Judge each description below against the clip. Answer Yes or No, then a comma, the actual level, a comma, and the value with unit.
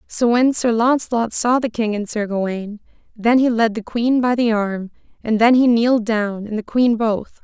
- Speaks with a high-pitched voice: Yes, high, 225 Hz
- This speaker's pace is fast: Yes, fast, 220 wpm